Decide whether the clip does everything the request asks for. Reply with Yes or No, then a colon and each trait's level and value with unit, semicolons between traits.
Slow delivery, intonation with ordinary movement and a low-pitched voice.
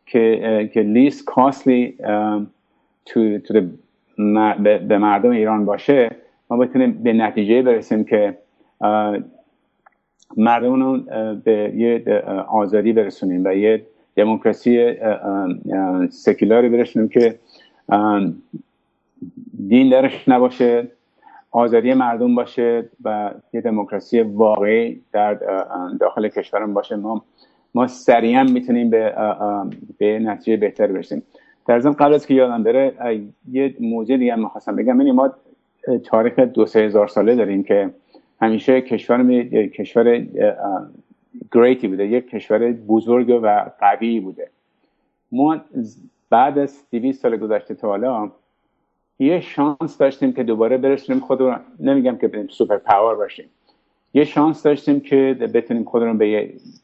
Yes: slow, 120 wpm; average, 3.7 semitones; low, 120 Hz